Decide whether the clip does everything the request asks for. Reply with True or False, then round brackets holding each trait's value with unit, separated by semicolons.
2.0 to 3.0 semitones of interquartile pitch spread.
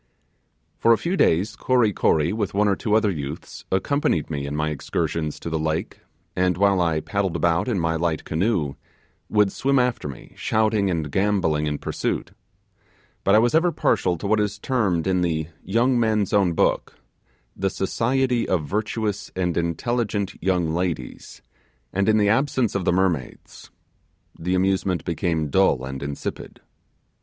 False (4.8 semitones)